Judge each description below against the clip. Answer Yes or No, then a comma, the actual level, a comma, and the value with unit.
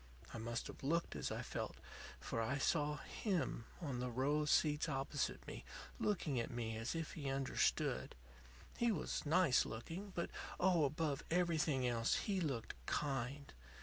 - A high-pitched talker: No, medium, 145 Hz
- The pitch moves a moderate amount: Yes, average, 4.7 semitones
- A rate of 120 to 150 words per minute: No, average, 160 wpm